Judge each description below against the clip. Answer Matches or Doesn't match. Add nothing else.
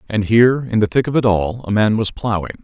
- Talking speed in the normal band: Doesn't match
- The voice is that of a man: Matches